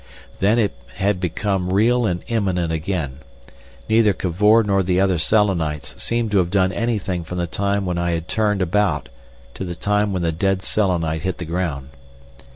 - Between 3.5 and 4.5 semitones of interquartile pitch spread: No, average, 3.0 semitones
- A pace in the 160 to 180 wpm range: Yes, average, 175 wpm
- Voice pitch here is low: Yes, very low, 95 Hz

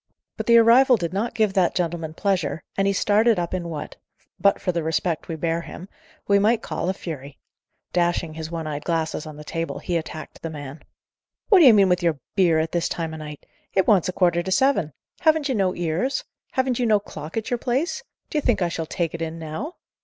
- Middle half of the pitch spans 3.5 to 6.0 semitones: Yes, average, 4.8 semitones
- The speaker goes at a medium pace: No, fast, 225 wpm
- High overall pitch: No, medium, 175 Hz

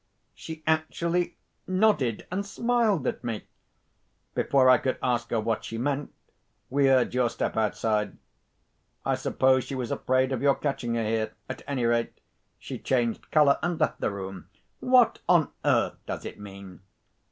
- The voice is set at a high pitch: No, low, 130 Hz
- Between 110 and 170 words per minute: Yes, average, 160 wpm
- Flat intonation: No, wide, 5.4 semitones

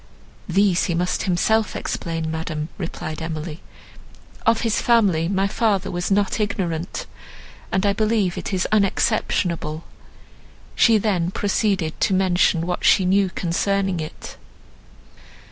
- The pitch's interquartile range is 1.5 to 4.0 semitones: Yes, average, 3.2 semitones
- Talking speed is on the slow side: Yes, slow, 125 wpm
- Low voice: No, medium, 185 Hz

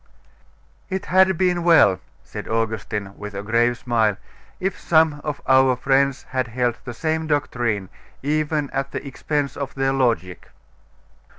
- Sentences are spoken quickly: No, average, 140 wpm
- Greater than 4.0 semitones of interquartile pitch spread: Yes, average, 4.9 semitones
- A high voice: No, low, 135 Hz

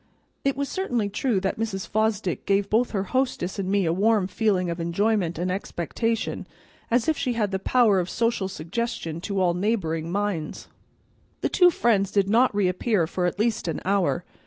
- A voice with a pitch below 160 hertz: No, high, 200 Hz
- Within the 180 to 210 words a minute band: Yes, average, 185 wpm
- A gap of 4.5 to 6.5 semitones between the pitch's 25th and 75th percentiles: No, average, 3.8 semitones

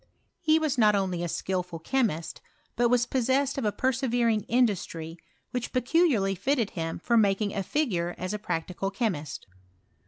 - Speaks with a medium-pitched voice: No, high, 215 Hz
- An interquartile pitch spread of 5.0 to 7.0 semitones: Yes, wide, 5.6 semitones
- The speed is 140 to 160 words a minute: Yes, average, 155 wpm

